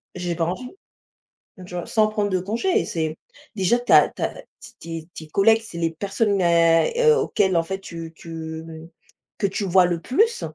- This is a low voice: No, medium, 185 Hz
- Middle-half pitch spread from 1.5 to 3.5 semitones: No, average, 4.4 semitones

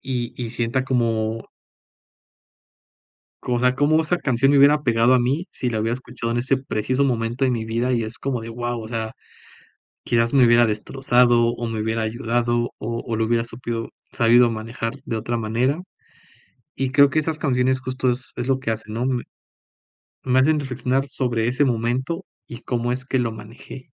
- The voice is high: No, low, 120 Hz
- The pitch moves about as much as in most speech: No, narrow, 2.2 semitones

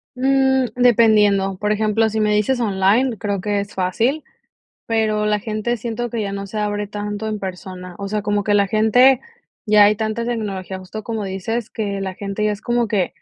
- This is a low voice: No, high, 210 Hz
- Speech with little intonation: Yes, narrow, 2.2 semitones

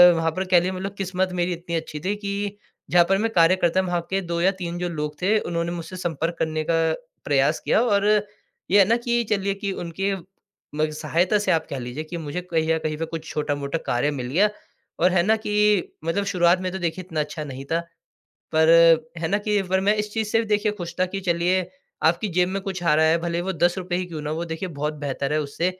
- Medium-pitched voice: Yes, medium, 175 Hz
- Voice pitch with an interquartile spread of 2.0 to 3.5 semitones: Yes, average, 3.2 semitones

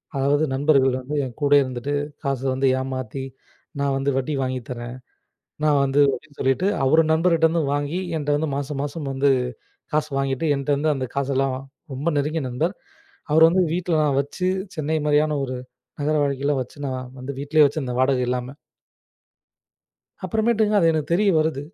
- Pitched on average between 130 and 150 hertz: Yes, medium, 140 Hz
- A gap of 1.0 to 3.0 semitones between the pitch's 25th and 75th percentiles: Yes, average, 2.7 semitones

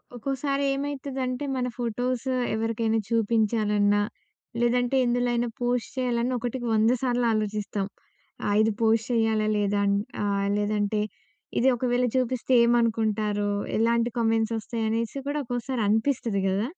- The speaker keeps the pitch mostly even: Yes, narrow, 2.3 semitones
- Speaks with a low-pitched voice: No, high, 230 Hz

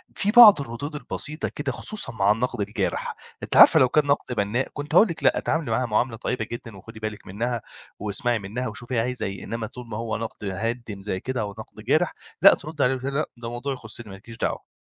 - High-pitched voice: No, low, 120 Hz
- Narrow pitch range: No, average, 3.8 semitones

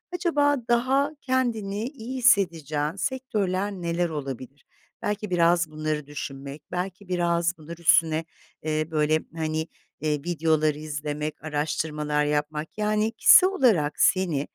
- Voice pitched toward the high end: No, medium, 170 Hz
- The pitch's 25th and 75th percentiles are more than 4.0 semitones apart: Yes, wide, 5.5 semitones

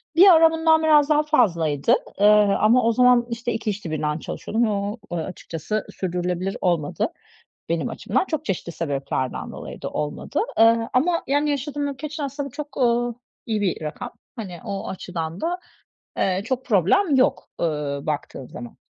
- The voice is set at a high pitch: Yes, high, 220 Hz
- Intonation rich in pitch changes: Yes, wide, 8.7 semitones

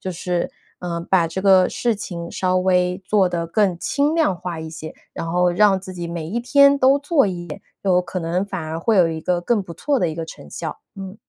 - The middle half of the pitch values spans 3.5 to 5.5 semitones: No, average, 3.0 semitones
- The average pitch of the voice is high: No, medium, 180 Hz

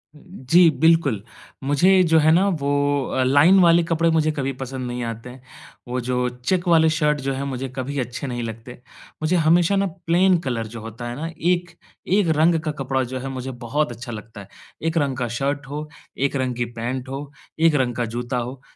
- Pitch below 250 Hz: Yes, low, 135 Hz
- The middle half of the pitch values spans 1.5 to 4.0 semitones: No, average, 4.6 semitones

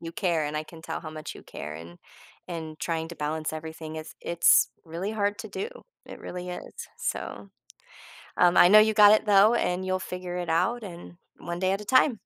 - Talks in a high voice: No, medium, 175 Hz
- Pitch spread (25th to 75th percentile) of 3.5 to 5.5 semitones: Yes, average, 4.1 semitones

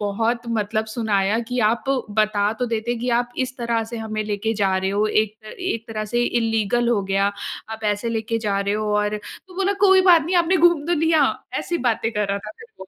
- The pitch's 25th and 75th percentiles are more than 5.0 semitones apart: No, average, 2.8 semitones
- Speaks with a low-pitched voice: No, high, 225 Hz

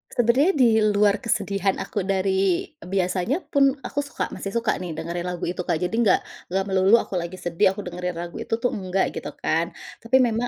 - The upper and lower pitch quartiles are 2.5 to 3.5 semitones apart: No, average, 3.9 semitones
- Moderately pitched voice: No, high, 195 Hz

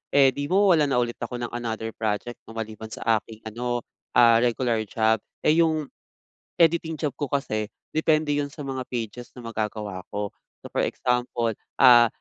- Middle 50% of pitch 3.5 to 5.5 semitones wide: Yes, average, 4.1 semitones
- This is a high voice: No, low, 120 Hz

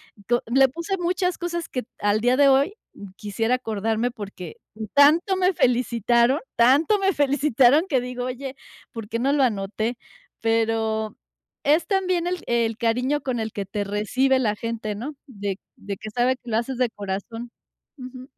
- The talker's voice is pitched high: Yes, high, 245 Hz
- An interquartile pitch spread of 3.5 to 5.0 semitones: Yes, average, 4.2 semitones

